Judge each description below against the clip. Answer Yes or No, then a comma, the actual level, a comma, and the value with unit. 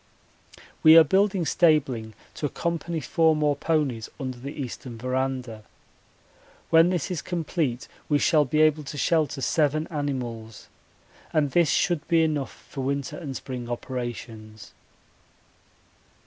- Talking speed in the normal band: No, slow, 130 wpm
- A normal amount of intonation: Yes, average, 4.1 semitones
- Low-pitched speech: No, medium, 145 Hz